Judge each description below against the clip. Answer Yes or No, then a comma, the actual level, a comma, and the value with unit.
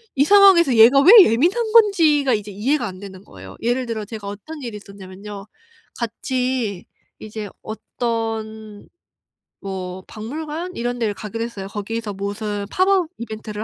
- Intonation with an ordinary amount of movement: Yes, average, 4.5 semitones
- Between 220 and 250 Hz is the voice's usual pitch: Yes, high, 225 Hz